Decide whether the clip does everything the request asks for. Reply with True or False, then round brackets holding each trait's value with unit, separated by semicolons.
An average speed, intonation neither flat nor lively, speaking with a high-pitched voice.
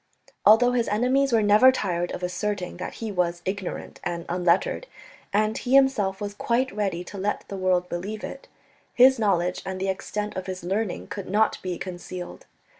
True (180 wpm; 3.3 semitones; 200 Hz)